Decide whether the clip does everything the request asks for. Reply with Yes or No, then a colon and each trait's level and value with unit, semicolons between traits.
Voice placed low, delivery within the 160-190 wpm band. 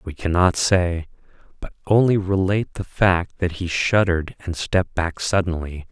No: very low, 90 Hz; average, 150 wpm